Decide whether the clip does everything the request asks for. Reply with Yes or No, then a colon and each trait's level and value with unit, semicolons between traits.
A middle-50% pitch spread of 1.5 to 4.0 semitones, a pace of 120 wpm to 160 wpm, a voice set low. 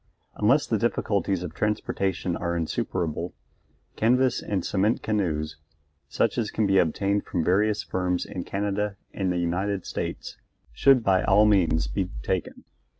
Yes: average, 3.1 semitones; average, 145 wpm; very low, 95 Hz